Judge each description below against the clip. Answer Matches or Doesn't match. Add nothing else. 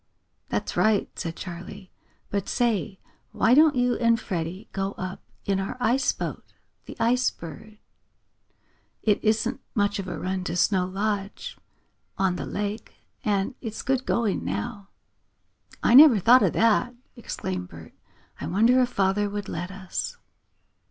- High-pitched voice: Matches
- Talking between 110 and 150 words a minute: Matches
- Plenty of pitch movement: Doesn't match